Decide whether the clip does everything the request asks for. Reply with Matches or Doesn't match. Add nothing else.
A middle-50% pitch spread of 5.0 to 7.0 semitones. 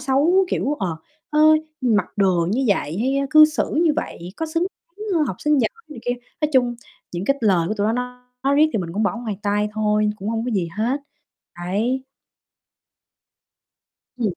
Matches